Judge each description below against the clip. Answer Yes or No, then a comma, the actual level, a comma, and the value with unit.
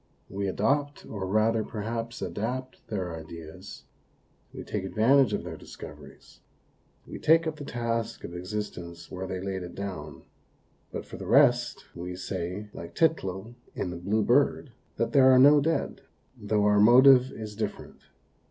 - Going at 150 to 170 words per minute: Yes, average, 160 wpm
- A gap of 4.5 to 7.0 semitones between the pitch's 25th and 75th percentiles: Yes, average, 5.2 semitones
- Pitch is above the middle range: No, low, 105 Hz